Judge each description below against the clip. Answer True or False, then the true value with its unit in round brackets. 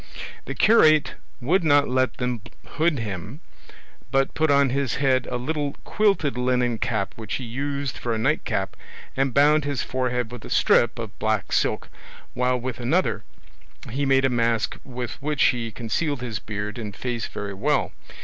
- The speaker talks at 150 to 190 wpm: True (170 wpm)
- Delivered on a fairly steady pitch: False (3.4 semitones)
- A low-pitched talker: True (125 Hz)